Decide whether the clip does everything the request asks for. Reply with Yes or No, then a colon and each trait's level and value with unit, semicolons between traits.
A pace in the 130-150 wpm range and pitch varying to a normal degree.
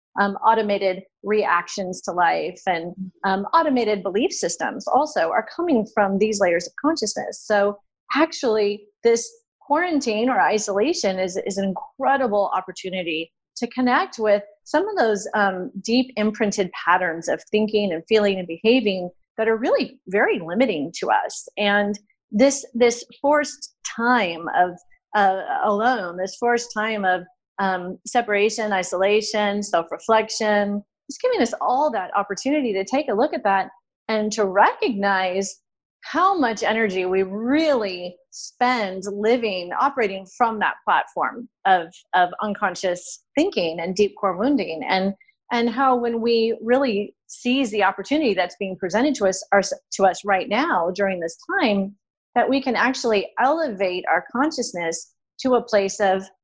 Yes: average, 140 wpm; average, 4.5 semitones